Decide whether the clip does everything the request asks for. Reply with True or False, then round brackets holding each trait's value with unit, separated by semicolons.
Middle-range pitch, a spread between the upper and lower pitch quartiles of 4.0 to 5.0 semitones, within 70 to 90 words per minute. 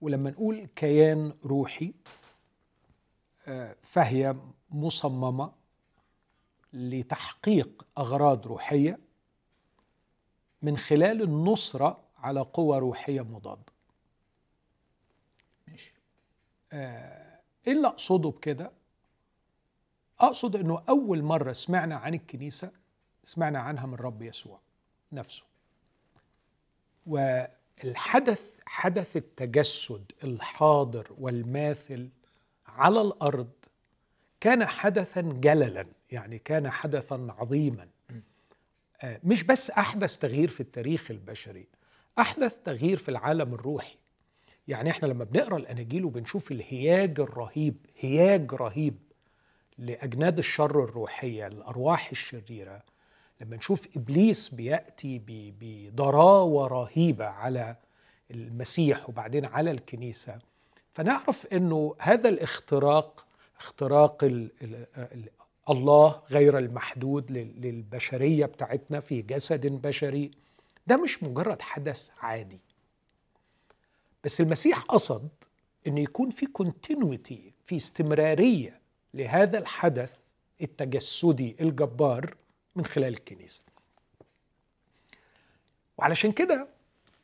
True (145 Hz; 4.7 semitones; 85 wpm)